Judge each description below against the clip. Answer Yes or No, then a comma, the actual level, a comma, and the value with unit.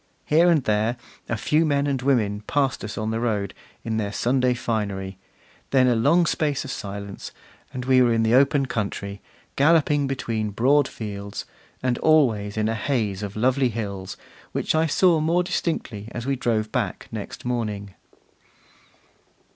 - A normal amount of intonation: Yes, average, 4.8 semitones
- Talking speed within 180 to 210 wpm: No, average, 165 wpm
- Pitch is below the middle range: Yes, low, 120 Hz